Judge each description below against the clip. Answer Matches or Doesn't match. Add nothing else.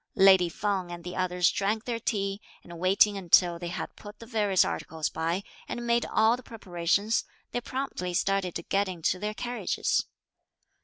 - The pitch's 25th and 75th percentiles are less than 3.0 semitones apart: Doesn't match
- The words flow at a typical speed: Matches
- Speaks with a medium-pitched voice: Doesn't match